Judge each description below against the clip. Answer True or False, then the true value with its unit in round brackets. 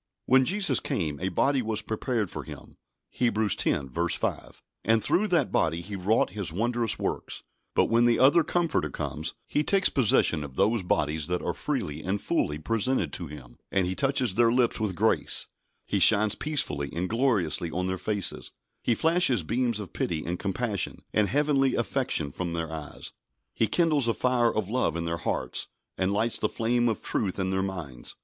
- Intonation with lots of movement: True (6.2 semitones)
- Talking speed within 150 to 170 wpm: False (185 wpm)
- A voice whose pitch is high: False (105 Hz)